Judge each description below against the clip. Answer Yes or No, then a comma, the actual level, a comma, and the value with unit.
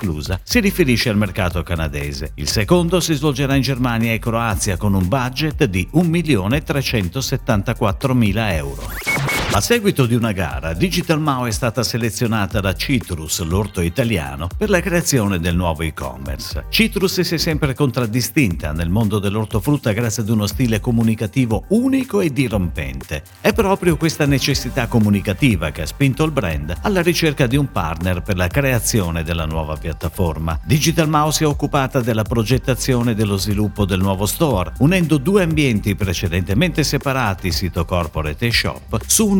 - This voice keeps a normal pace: Yes, average, 155 wpm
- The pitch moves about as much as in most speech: No, wide, 7.4 semitones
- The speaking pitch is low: Yes, low, 115 Hz